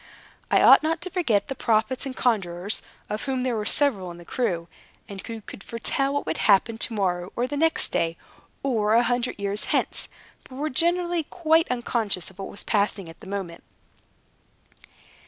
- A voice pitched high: Yes, high, 225 Hz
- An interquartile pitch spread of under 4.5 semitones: No, wide, 5.6 semitones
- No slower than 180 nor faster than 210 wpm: Yes, average, 185 wpm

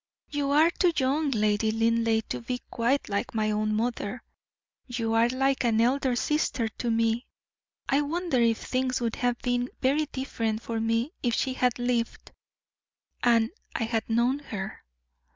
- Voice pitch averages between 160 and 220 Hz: No, high, 240 Hz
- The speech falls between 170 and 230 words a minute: No, average, 160 wpm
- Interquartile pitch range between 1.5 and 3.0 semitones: Yes, average, 2.7 semitones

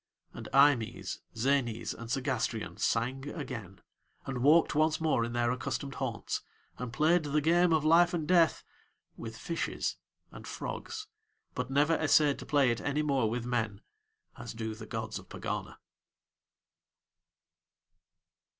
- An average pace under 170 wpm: Yes, average, 140 wpm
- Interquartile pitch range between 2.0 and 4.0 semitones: No, average, 4.7 semitones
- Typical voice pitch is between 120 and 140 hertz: Yes, low, 135 Hz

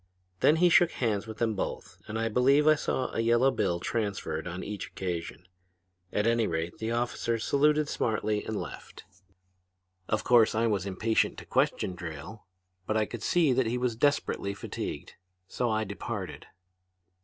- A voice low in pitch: Yes, low, 110 Hz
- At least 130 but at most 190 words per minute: Yes, average, 165 wpm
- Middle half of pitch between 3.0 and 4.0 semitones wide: Yes, average, 3.6 semitones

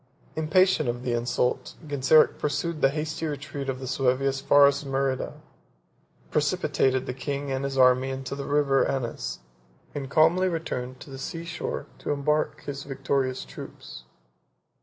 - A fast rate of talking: No, average, 155 wpm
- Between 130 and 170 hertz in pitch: Yes, medium, 140 Hz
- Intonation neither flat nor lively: No, narrow, 2.2 semitones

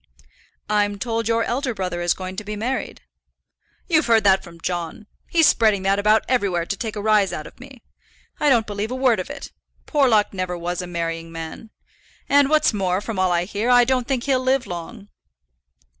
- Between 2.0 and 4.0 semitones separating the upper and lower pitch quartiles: No, average, 4.9 semitones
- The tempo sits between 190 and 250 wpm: Yes, average, 200 wpm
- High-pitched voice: Yes, high, 210 Hz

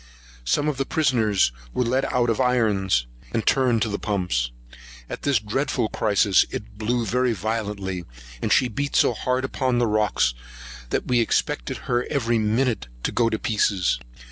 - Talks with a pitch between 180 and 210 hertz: No, low, 115 Hz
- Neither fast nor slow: Yes, average, 170 wpm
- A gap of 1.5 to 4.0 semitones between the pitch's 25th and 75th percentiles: Yes, average, 3.5 semitones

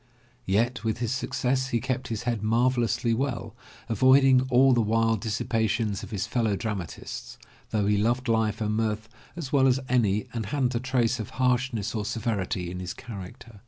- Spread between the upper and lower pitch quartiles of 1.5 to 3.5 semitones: Yes, average, 2.9 semitones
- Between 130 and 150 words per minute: No, average, 180 wpm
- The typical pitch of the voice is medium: No, low, 115 Hz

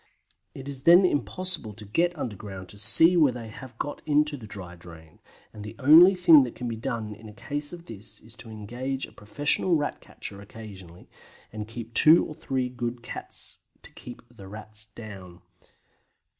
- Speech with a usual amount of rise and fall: No, wide, 5.7 semitones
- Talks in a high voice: No, low, 115 Hz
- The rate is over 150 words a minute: Yes, average, 185 wpm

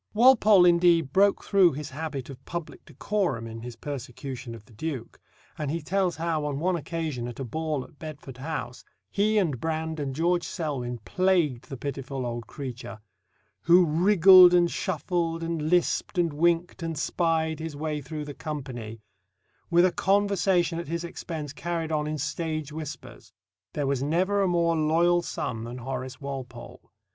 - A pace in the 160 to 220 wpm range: Yes, average, 165 wpm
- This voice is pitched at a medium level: Yes, medium, 155 Hz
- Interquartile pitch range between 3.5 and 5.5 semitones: Yes, average, 4.1 semitones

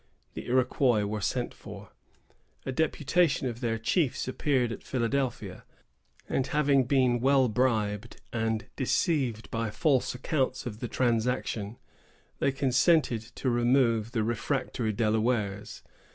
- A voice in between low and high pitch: No, low, 120 Hz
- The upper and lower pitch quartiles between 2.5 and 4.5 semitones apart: Yes, average, 3.0 semitones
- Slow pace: Yes, slow, 125 wpm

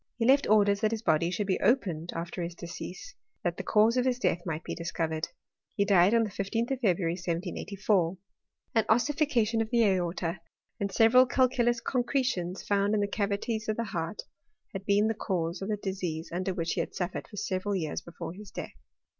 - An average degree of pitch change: Yes, average, 4.4 semitones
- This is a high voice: Yes, high, 200 Hz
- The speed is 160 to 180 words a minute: No, fast, 205 wpm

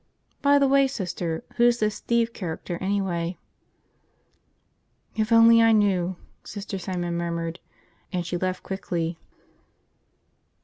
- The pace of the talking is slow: Yes, slow, 115 wpm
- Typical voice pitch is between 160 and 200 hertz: Yes, high, 190 Hz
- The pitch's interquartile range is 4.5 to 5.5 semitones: Yes, average, 4.8 semitones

